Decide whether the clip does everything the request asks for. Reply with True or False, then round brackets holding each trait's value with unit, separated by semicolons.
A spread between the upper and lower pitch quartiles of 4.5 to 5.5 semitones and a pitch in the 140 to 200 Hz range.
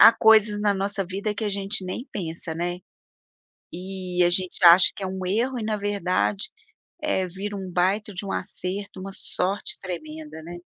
False (2.4 semitones; 190 Hz)